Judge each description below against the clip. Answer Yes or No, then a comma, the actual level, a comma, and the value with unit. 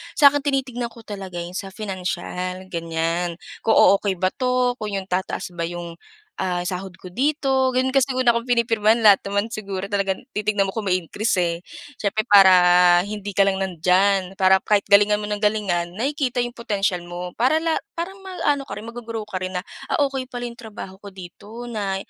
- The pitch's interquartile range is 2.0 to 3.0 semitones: No, average, 4.3 semitones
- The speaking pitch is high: Yes, high, 205 Hz